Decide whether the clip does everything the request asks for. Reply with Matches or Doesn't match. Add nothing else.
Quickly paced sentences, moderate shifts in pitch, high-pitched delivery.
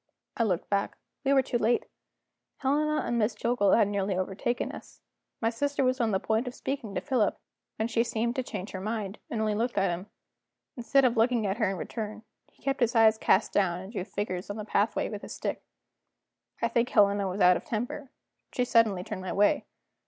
Matches